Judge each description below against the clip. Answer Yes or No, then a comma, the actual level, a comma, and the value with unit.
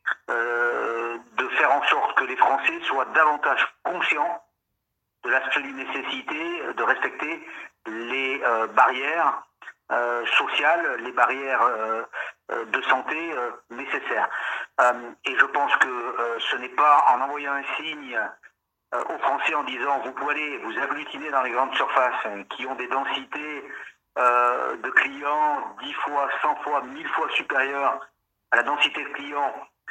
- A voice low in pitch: Yes, low, 120 Hz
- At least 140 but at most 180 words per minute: Yes, average, 150 wpm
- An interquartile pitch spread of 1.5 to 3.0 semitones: Yes, narrow, 2.4 semitones